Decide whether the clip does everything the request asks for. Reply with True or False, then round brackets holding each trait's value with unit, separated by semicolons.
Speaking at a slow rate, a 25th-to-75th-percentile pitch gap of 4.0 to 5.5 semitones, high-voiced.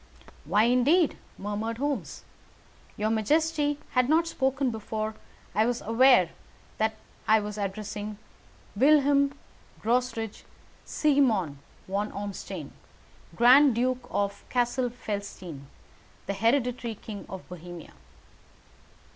True (100 wpm; 4.4 semitones; 225 Hz)